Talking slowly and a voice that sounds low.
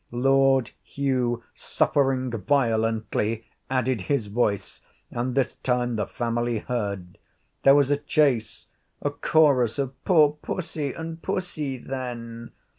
Yes: slow, 115 wpm; low, 130 Hz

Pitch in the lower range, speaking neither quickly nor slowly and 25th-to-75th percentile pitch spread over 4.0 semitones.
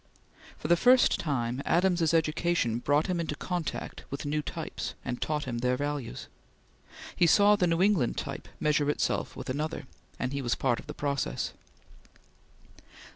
No: medium, 150 Hz; average, 160 wpm; average, 4.6 semitones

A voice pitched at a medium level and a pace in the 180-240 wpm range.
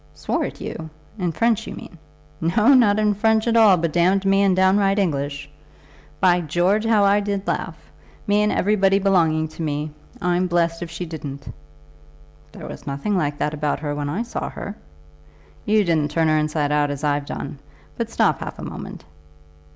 Yes: medium, 175 Hz; average, 185 wpm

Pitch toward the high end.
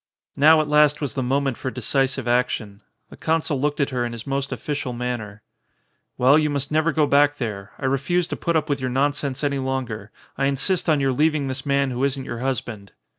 No: low, 135 Hz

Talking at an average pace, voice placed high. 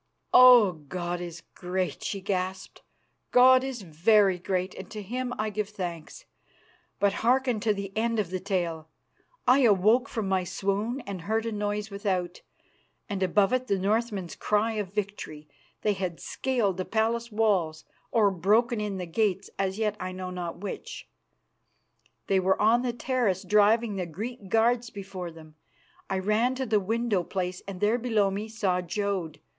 Yes: average, 165 wpm; high, 200 Hz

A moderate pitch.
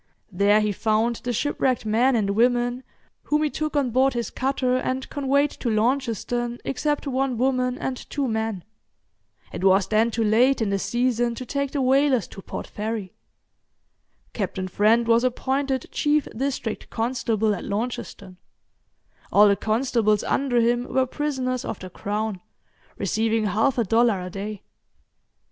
No: high, 235 Hz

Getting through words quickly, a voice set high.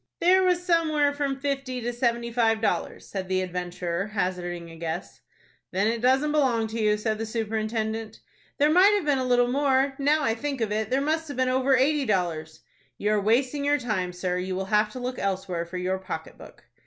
Yes: fast, 210 wpm; high, 230 Hz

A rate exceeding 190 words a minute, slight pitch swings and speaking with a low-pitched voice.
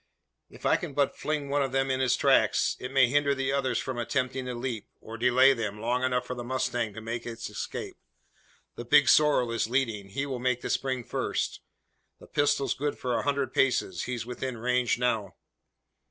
Yes: average, 200 wpm; narrow, 2.2 semitones; low, 125 Hz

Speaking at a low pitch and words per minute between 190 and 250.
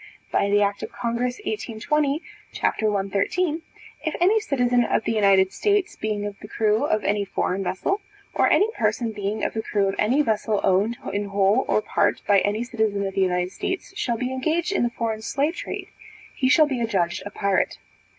No: high, 220 Hz; average, 195 wpm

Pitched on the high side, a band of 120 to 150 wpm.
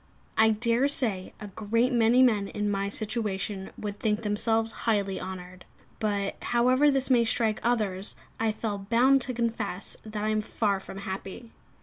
No: high, 215 Hz; average, 160 wpm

